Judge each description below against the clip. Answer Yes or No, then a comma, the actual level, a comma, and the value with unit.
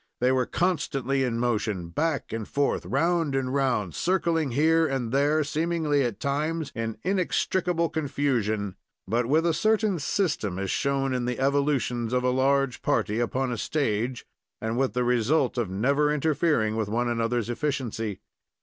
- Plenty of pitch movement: No, average, 4.5 semitones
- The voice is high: No, low, 135 Hz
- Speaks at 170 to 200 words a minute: No, average, 160 wpm